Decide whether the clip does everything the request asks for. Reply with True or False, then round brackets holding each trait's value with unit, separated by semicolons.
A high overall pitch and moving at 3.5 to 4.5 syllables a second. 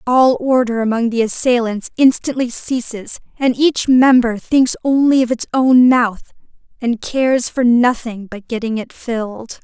True (245 Hz; 4.4 syllables/s)